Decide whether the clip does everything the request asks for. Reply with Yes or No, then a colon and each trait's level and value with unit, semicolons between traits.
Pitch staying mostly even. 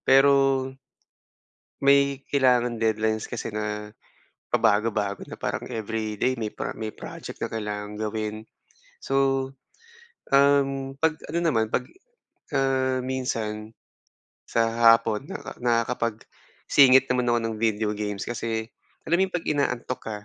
No: average, 3.7 semitones